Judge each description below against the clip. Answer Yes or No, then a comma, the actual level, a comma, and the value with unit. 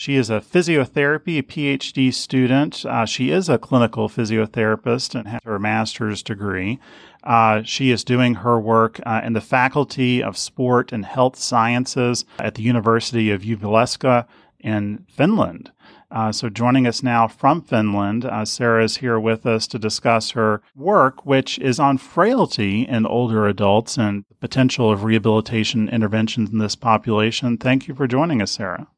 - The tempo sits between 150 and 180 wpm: Yes, average, 160 wpm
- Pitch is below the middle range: Yes, low, 115 Hz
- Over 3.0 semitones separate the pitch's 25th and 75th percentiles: No, average, 2.7 semitones